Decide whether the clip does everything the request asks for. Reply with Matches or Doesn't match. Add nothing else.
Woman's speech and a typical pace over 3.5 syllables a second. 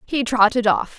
Matches